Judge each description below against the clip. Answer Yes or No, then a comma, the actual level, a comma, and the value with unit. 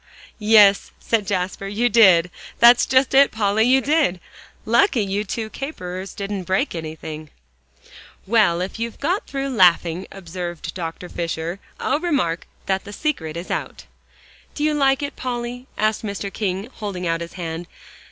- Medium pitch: No, high, 200 Hz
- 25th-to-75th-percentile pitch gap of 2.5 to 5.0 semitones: No, wide, 5.4 semitones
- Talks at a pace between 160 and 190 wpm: No, average, 150 wpm